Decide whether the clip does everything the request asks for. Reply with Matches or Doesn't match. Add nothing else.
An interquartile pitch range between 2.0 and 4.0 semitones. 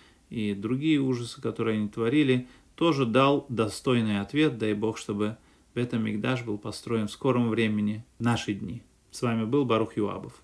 Matches